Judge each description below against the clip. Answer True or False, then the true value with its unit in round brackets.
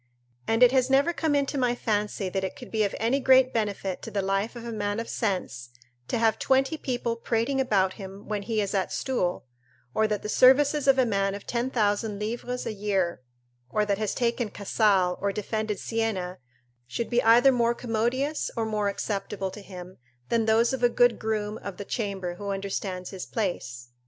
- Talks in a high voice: True (215 Hz)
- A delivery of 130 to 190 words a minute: False (200 wpm)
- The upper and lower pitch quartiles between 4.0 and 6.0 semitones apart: False (3.5 semitones)